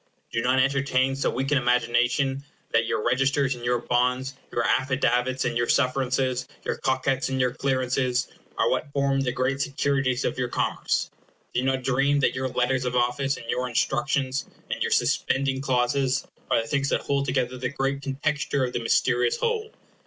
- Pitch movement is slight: Yes, narrow, 1.7 semitones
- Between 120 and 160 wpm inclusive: No, average, 180 wpm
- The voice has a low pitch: Yes, low, 130 Hz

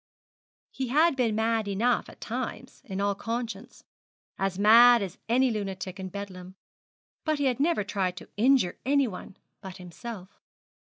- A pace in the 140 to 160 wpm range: Yes, average, 155 wpm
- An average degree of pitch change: Yes, average, 4.2 semitones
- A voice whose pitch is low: No, high, 215 Hz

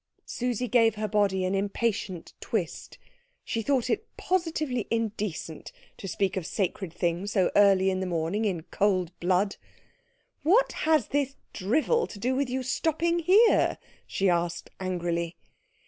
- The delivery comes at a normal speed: Yes, average, 145 wpm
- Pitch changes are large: Yes, wide, 5.9 semitones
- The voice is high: Yes, high, 205 Hz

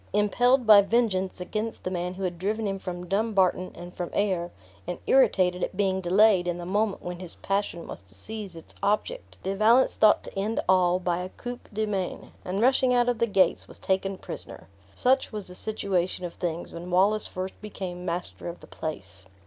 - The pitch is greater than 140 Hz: Yes, high, 190 Hz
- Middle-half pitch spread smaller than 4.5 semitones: Yes, average, 3.2 semitones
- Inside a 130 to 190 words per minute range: No, average, 200 wpm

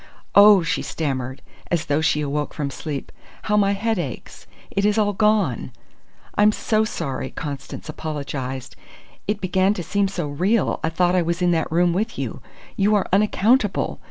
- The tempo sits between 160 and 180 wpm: Yes, average, 170 wpm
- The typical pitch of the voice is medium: Yes, medium, 180 Hz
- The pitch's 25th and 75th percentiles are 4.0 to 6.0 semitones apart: Yes, wide, 5.6 semitones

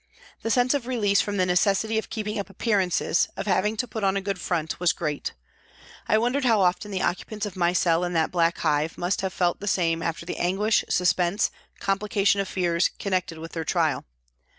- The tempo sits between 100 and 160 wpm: No, fast, 205 wpm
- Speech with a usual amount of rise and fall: Yes, average, 3.2 semitones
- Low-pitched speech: No, high, 190 Hz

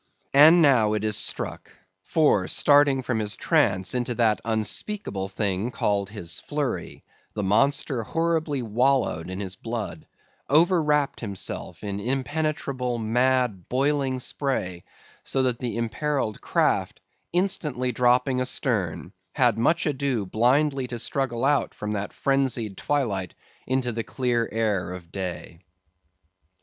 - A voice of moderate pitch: No, low, 120 Hz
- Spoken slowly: Yes, slow, 130 wpm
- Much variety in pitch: No, average, 4.7 semitones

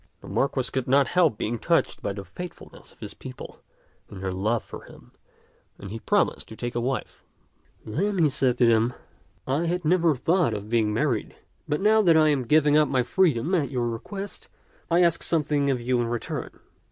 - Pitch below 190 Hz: Yes, low, 135 Hz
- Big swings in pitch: Yes, wide, 5.9 semitones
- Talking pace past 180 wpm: Yes, average, 200 wpm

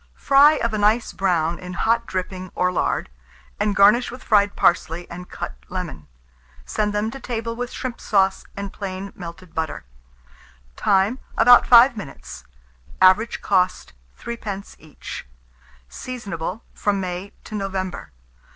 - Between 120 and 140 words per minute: Yes, slow, 135 wpm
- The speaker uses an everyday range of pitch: Yes, average, 3.8 semitones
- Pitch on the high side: Yes, high, 200 Hz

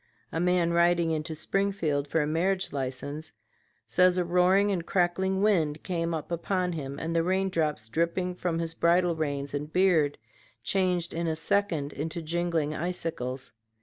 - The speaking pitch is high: No, medium, 170 Hz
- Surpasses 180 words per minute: No, average, 155 wpm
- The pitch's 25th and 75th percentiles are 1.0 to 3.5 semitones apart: Yes, average, 2.8 semitones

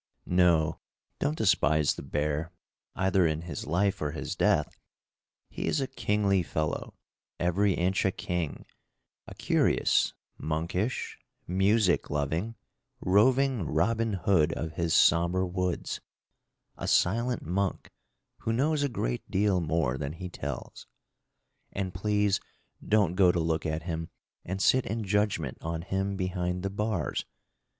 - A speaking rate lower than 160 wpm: Yes, slow, 135 wpm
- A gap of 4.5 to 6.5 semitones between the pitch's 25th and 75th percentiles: No, average, 3.9 semitones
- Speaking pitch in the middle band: No, very low, 90 Hz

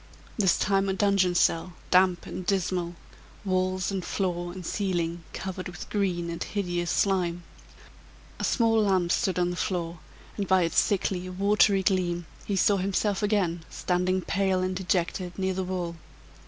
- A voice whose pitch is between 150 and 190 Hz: Yes, medium, 185 Hz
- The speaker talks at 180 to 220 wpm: No, average, 155 wpm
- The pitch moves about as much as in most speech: No, narrow, 1.8 semitones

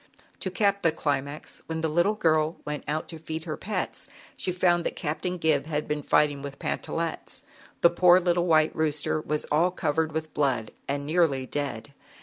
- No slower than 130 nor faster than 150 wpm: No, average, 175 wpm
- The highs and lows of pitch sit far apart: No, average, 2.7 semitones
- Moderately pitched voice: Yes, medium, 155 Hz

